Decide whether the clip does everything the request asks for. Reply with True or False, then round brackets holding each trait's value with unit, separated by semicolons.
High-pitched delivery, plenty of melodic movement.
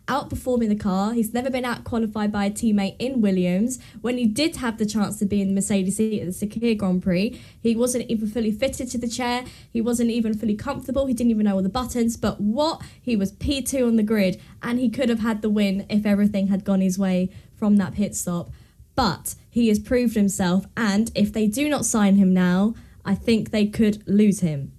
False (215 Hz; 3.1 semitones)